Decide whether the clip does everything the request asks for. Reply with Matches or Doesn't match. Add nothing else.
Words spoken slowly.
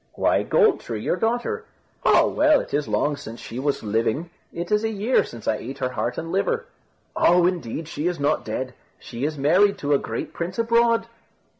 Doesn't match